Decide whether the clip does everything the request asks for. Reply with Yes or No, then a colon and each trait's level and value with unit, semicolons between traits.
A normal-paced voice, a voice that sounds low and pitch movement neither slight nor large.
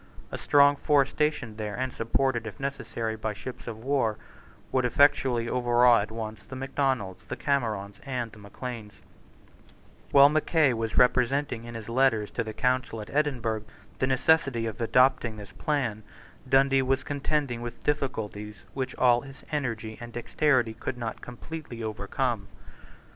Yes: average, 150 wpm; low, 120 Hz; average, 3.5 semitones